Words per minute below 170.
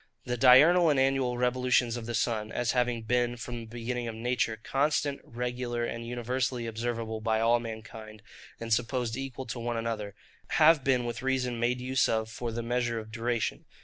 No: average, 180 wpm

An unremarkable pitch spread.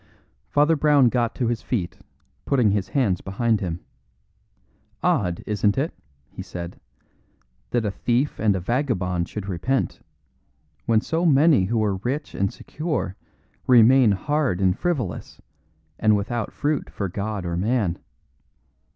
No: wide, 5.8 semitones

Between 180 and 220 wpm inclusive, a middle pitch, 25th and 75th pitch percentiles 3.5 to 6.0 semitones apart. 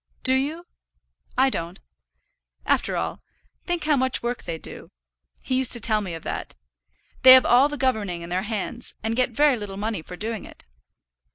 No: average, 185 wpm; high, 235 Hz; average, 4.6 semitones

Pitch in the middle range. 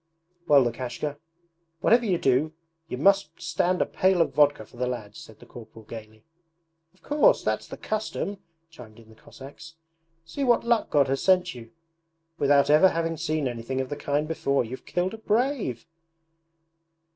Yes: medium, 145 Hz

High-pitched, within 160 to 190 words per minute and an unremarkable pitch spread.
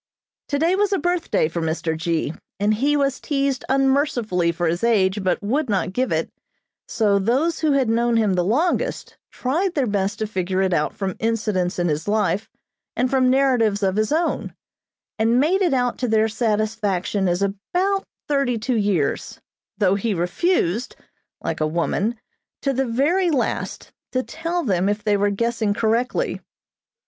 No: high, 225 Hz; average, 170 wpm; wide, 5.9 semitones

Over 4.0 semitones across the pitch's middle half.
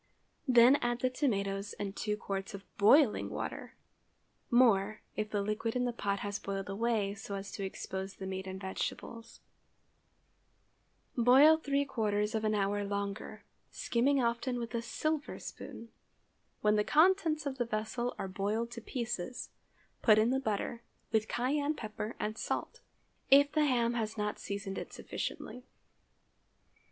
No: average, 3.6 semitones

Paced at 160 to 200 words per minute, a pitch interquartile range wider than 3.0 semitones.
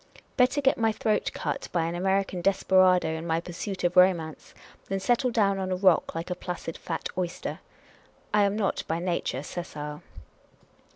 No: average, 170 wpm; average, 2.7 semitones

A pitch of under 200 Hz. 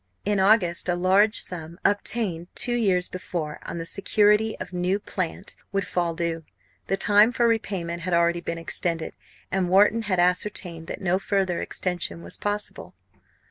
Yes: medium, 185 Hz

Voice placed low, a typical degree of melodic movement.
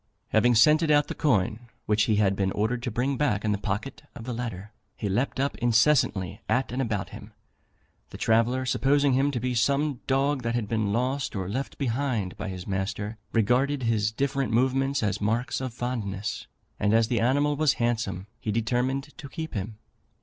Yes: low, 120 Hz; average, 4.2 semitones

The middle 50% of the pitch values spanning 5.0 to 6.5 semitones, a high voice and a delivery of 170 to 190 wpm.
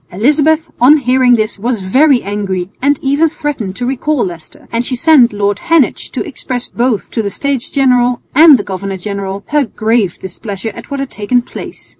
Yes: wide, 5.6 semitones; high, 245 Hz; average, 185 wpm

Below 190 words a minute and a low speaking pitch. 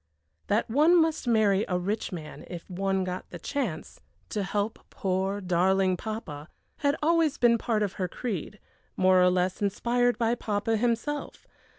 No: average, 160 wpm; high, 205 Hz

